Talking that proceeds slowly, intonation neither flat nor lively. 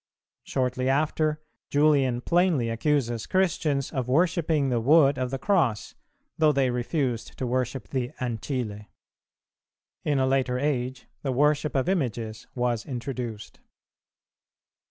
Yes: slow, 120 wpm; average, 3.4 semitones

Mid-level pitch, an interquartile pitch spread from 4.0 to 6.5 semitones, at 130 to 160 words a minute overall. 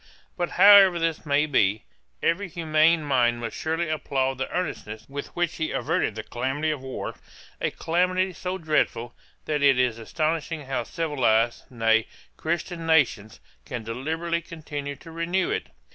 Yes: medium, 155 Hz; average, 4.7 semitones; average, 150 wpm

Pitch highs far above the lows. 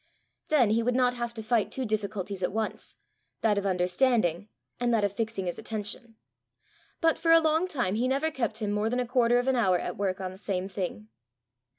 No: average, 3.9 semitones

